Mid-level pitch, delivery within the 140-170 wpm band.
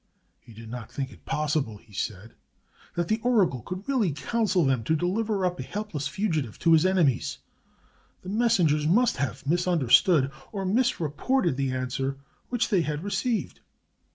Yes: medium, 165 Hz; average, 165 wpm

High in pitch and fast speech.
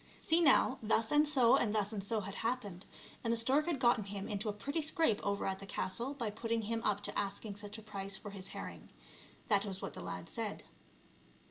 Yes: high, 215 Hz; fast, 225 wpm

